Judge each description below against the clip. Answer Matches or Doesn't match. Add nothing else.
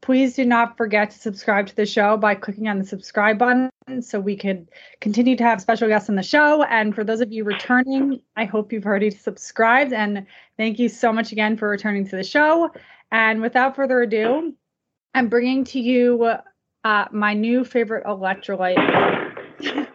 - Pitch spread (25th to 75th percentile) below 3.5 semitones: Matches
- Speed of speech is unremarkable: Matches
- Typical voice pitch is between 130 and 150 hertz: Doesn't match